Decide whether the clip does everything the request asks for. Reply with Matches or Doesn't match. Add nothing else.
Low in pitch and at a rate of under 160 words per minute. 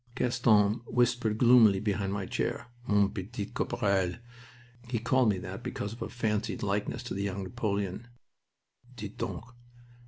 Matches